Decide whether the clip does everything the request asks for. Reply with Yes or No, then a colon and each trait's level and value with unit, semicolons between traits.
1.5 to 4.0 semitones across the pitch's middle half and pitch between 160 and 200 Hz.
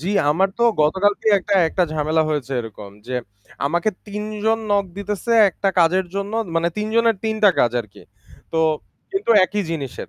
No: average, 5.3 semitones; high, 190 Hz